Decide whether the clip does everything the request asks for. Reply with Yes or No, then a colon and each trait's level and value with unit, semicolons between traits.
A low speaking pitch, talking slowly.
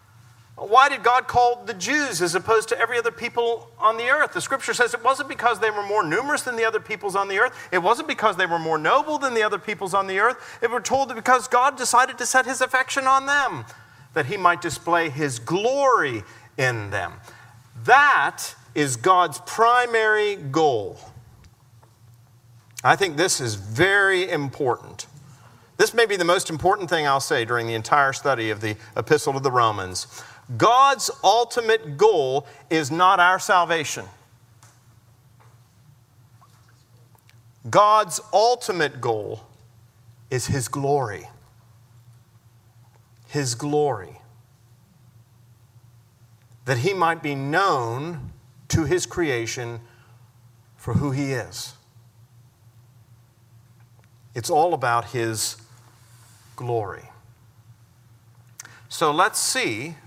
Yes: low, 130 Hz; slow, 130 wpm